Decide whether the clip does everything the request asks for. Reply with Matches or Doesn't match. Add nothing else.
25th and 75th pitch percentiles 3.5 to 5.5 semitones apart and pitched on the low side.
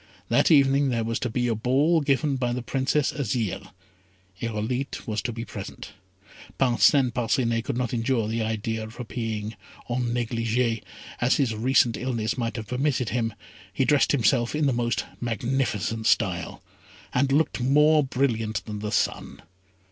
Doesn't match